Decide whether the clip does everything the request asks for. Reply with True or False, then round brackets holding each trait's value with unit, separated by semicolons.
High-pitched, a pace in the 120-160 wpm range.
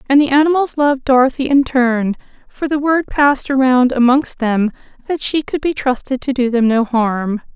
False (260 Hz; 190 wpm)